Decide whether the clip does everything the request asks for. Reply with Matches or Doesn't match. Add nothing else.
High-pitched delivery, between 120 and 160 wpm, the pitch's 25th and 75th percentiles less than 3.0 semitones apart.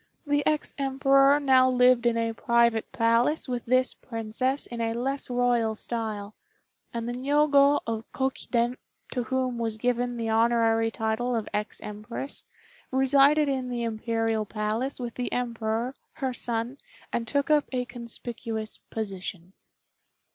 Matches